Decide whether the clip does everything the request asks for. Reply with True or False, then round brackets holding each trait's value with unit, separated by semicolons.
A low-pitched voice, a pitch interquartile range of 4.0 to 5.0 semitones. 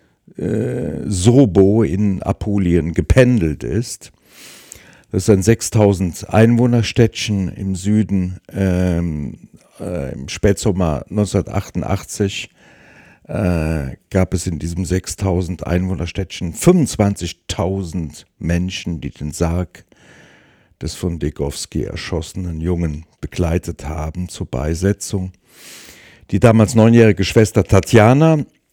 False (95 Hz; 3.4 semitones)